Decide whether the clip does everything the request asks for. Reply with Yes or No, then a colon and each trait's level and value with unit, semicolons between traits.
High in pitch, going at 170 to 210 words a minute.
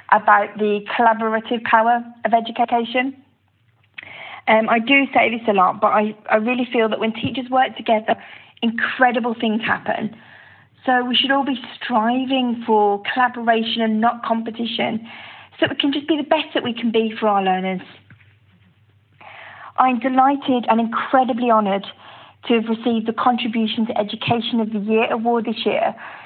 No: high, 230 Hz; average, 160 wpm